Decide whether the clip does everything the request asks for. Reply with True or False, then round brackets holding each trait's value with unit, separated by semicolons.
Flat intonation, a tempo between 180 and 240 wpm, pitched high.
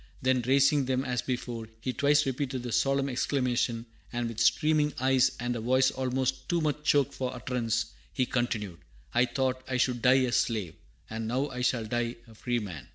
False (2.1 semitones; 190 wpm; 125 Hz)